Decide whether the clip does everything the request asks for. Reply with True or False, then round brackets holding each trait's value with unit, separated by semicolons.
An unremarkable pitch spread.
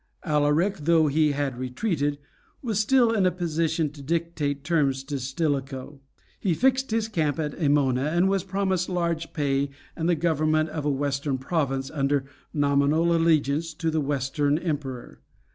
True (3.2 semitones)